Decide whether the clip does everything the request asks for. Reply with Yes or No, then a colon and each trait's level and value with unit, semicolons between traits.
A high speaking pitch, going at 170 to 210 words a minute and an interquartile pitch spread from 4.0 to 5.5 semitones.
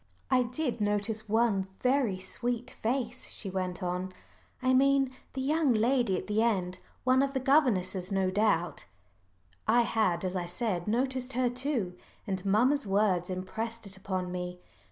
No: high, 220 Hz; average, 155 wpm; average, 5.2 semitones